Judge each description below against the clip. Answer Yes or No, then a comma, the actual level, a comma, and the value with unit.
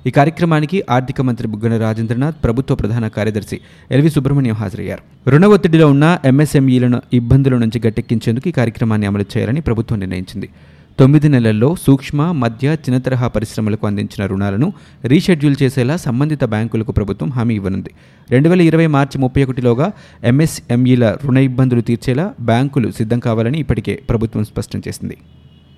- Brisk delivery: Yes, fast, 135 wpm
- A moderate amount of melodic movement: Yes, average, 4.2 semitones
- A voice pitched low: Yes, low, 120 Hz